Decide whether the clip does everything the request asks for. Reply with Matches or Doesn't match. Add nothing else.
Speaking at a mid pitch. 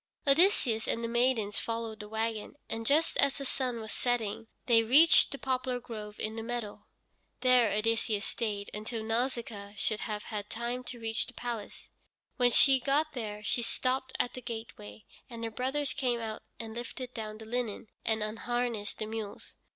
Doesn't match